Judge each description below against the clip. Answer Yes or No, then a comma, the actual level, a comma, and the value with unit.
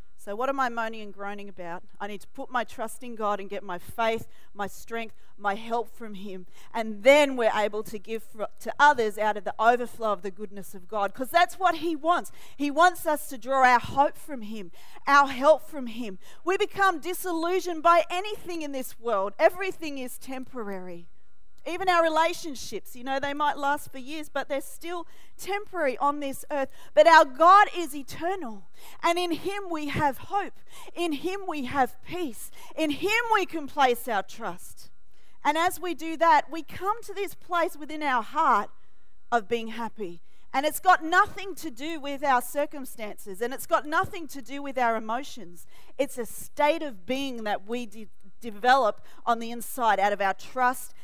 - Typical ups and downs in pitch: No, wide, 6.6 semitones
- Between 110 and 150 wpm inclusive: No, average, 190 wpm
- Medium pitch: No, very high, 275 Hz